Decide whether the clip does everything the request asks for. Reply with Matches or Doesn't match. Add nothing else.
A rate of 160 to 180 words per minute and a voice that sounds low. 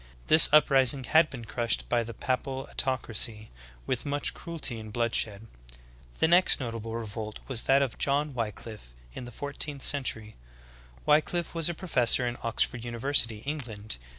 Doesn't match